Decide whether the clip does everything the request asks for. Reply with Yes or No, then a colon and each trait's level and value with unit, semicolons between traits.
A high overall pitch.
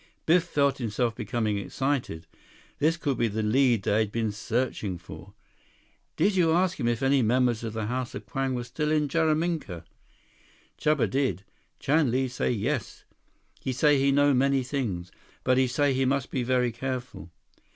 No: low, 130 Hz